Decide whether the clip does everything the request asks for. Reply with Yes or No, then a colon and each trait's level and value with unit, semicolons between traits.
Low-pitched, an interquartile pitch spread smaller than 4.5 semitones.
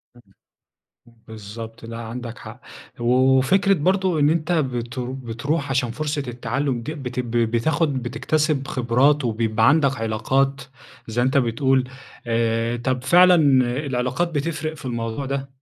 Yes: low, 130 Hz; average, 3.7 semitones